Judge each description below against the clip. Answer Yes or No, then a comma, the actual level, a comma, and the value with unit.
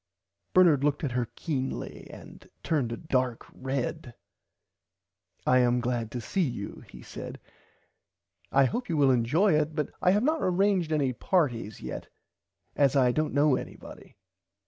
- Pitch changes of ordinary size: Yes, average, 4.7 semitones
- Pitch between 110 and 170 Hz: Yes, medium, 140 Hz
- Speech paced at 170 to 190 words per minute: No, average, 150 wpm